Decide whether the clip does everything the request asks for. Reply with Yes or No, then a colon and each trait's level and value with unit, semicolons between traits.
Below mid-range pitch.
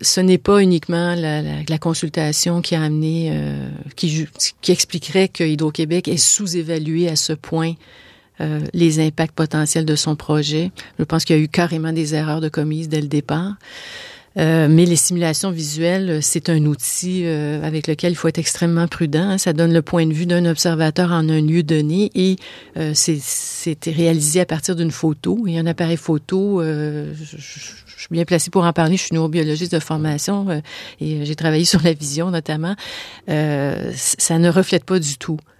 No: medium, 165 Hz